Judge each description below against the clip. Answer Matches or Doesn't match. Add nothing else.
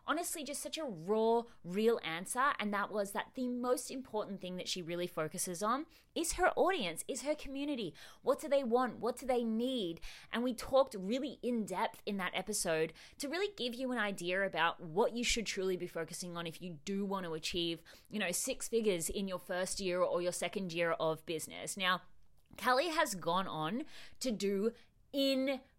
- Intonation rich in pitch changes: Matches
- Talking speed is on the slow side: Doesn't match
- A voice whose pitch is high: Matches